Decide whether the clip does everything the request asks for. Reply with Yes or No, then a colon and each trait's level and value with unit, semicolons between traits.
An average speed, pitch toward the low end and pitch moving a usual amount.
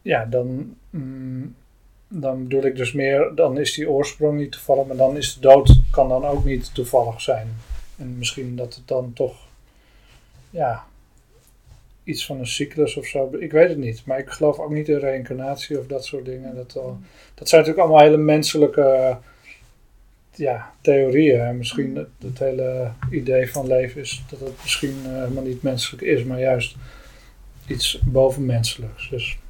No: average, 175 wpm; low, 130 Hz; narrow, 1.9 semitones